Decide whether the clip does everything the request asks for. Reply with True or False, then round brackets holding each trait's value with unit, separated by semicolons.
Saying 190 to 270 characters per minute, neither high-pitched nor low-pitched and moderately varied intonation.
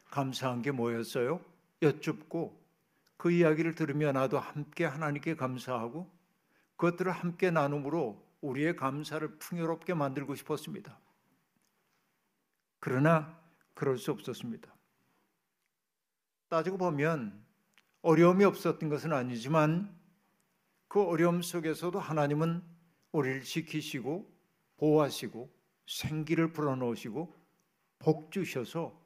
True (260 characters per minute; 160 Hz; 3.1 semitones)